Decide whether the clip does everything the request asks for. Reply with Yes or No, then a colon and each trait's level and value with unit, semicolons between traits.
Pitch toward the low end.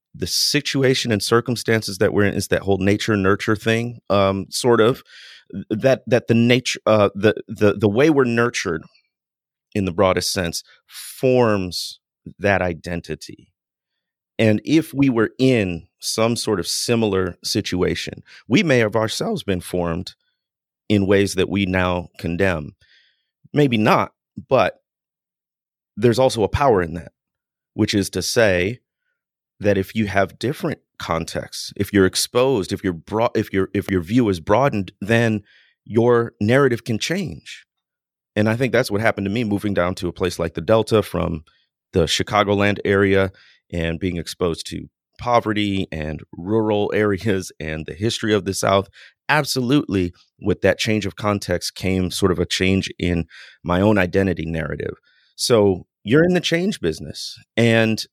Yes: low, 100 Hz